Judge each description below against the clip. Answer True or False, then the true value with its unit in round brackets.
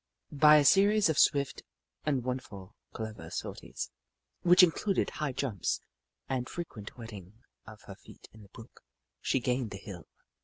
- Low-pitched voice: True (130 Hz)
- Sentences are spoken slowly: False (155 wpm)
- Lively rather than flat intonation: True (5.9 semitones)